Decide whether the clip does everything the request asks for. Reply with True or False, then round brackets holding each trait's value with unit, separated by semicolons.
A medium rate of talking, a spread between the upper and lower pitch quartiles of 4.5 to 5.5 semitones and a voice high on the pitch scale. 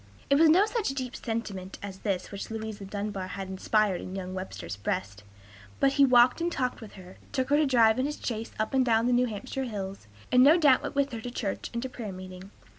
False (235 wpm; 5.2 semitones; 225 Hz)